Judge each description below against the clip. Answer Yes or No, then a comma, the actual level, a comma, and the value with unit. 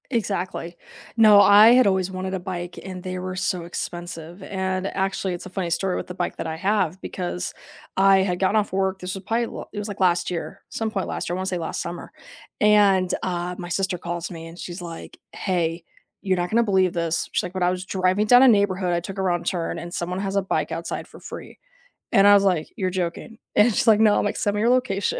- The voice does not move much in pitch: Yes, narrow, 2.3 semitones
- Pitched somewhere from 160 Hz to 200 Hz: Yes, medium, 185 Hz